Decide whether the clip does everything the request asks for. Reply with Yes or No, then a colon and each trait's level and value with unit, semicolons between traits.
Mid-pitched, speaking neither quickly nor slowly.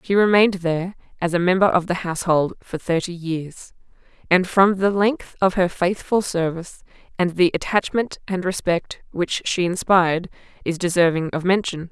Yes: medium, 180 Hz; average, 160 wpm